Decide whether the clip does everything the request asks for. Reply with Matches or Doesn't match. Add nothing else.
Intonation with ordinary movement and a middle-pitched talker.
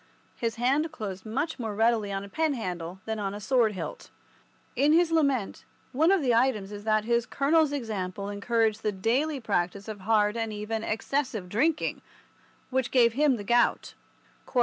Doesn't match